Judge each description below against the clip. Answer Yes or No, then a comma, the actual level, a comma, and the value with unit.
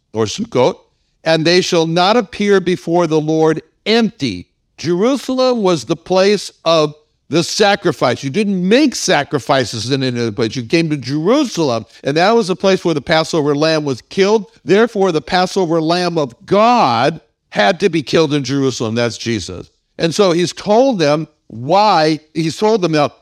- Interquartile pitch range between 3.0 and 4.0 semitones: No, average, 4.9 semitones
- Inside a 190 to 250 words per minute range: No, average, 170 wpm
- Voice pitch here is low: No, medium, 165 Hz